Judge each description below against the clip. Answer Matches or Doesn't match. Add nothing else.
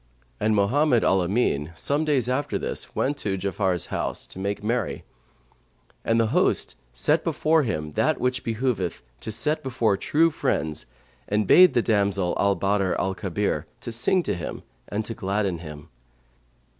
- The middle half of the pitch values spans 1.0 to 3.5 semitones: Doesn't match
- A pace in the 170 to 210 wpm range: Doesn't match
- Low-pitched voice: Matches